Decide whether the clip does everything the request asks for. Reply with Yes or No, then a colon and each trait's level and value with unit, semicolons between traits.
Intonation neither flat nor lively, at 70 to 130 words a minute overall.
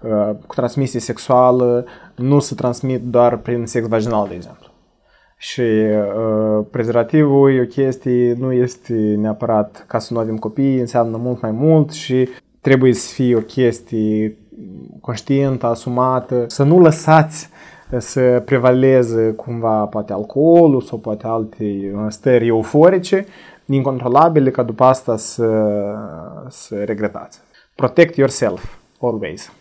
Yes: average, 3.2 semitones; average, 125 wpm